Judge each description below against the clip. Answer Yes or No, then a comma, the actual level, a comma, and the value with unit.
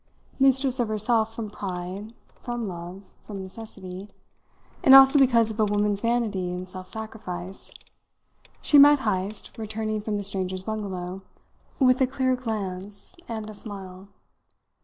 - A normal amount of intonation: Yes, average, 3.5 semitones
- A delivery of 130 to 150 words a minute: Yes, slow, 135 wpm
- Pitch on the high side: Yes, high, 210 Hz